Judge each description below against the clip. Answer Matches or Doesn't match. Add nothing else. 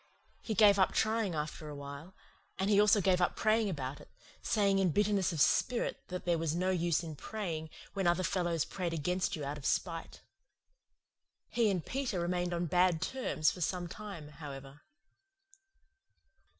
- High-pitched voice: Doesn't match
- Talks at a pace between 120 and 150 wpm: Doesn't match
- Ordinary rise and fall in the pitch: Matches